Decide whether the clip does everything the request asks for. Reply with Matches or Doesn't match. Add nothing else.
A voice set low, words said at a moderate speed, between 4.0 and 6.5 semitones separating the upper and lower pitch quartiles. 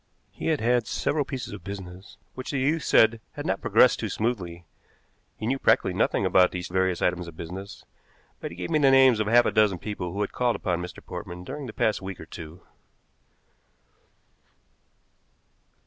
Matches